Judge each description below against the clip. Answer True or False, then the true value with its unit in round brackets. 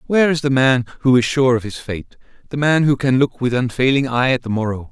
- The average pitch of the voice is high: False (130 Hz)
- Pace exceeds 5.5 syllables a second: True (5.9 syllables/s)